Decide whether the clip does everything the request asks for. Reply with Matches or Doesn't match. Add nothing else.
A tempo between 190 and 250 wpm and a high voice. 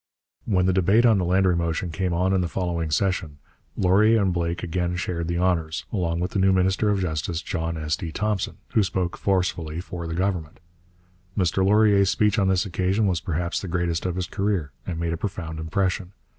Doesn't match